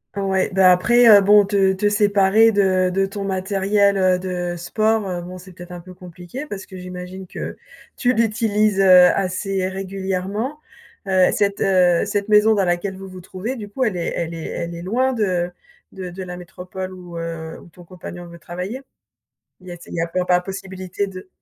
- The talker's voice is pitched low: No, high, 190 Hz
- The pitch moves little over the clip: Yes, narrow, 2.1 semitones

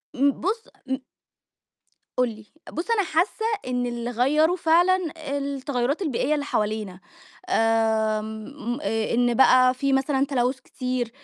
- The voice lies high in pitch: Yes, very high, 255 Hz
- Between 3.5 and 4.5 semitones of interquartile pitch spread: Yes, average, 4.2 semitones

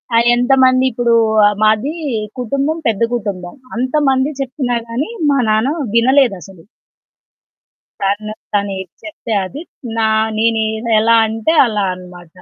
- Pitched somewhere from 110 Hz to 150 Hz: No, high, 230 Hz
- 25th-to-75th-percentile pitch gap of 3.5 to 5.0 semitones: Yes, average, 4.3 semitones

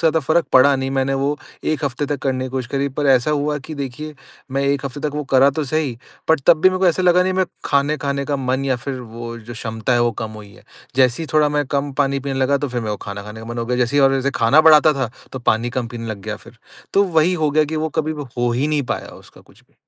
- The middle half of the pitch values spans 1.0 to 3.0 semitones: No, average, 3.4 semitones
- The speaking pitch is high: No, medium, 140 Hz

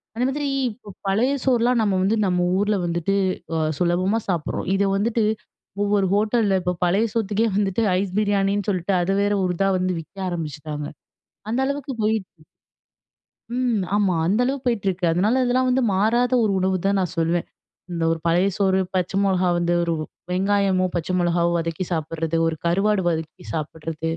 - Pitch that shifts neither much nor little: Yes, average, 3.5 semitones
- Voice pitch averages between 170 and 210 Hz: Yes, high, 195 Hz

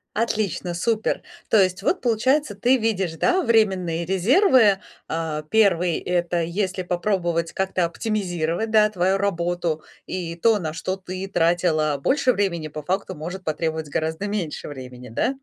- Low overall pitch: No, medium, 185 Hz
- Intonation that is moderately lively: Yes, average, 4.2 semitones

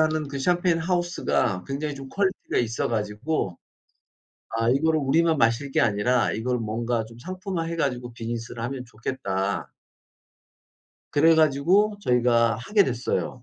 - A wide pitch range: Yes, wide, 5.8 semitones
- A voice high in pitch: No, low, 130 Hz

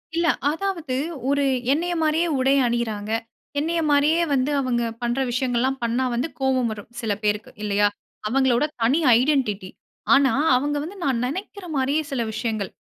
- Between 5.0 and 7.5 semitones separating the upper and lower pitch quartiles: No, average, 4.0 semitones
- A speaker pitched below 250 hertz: No, very high, 265 Hz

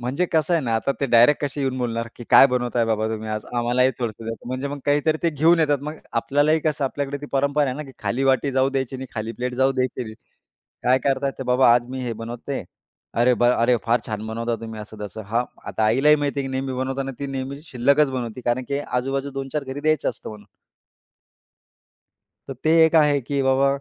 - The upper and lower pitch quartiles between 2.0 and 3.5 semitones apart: Yes, average, 2.9 semitones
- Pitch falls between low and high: No, low, 130 Hz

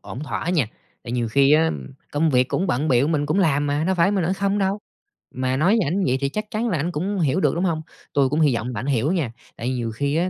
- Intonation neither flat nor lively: No, wide, 5.7 semitones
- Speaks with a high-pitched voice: No, medium, 150 Hz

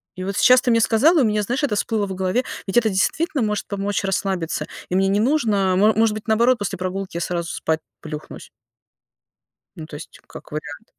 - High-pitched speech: Yes, high, 205 Hz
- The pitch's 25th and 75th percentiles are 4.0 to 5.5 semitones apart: No, average, 3.6 semitones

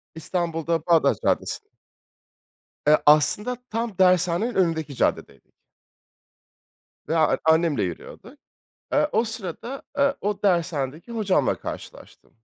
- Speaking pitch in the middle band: Yes, medium, 180 Hz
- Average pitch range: No, wide, 5.7 semitones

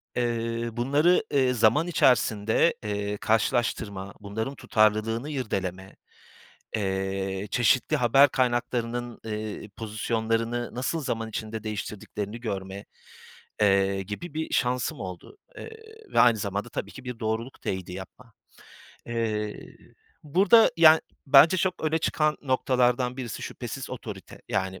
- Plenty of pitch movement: No, average, 3.8 semitones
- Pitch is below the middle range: Yes, low, 115 Hz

